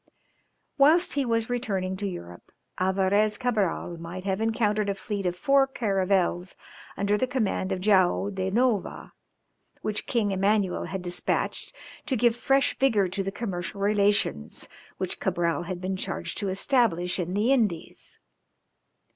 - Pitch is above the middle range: Yes, high, 200 Hz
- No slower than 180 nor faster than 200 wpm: No, average, 145 wpm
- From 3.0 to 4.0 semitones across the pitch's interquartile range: Yes, average, 3.4 semitones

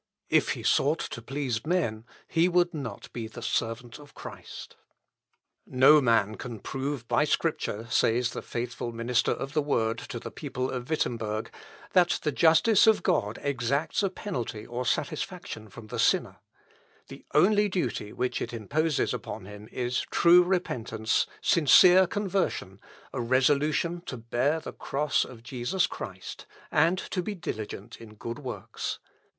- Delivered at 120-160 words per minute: Yes, average, 155 wpm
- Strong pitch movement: Yes, wide, 5.8 semitones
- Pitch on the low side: Yes, low, 130 Hz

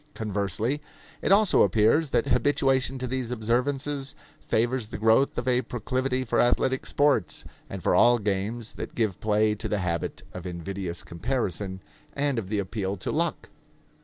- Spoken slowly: No, average, 160 wpm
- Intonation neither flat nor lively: Yes, average, 4.6 semitones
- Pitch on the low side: Yes, low, 115 Hz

